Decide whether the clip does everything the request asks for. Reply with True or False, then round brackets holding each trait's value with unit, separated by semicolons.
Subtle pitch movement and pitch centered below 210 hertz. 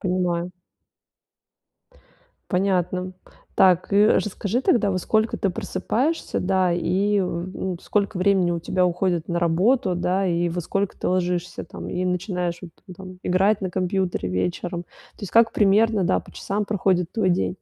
True (2.1 semitones; 185 Hz)